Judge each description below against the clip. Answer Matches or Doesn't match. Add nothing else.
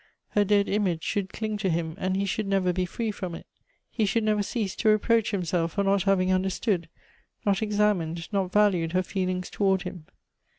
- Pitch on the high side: Matches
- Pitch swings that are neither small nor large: Doesn't match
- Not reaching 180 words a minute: Doesn't match